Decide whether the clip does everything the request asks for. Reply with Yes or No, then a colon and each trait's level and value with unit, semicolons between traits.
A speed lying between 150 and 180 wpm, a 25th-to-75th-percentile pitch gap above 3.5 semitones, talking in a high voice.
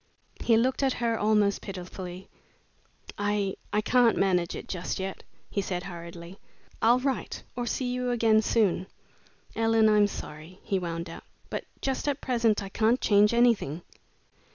Yes: average, 155 wpm; average, 4.1 semitones; high, 210 Hz